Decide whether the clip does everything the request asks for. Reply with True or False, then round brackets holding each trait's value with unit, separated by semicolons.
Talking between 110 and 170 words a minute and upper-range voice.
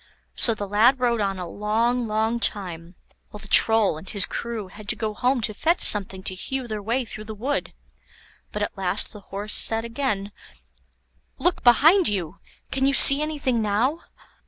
False (180 wpm; 220 Hz)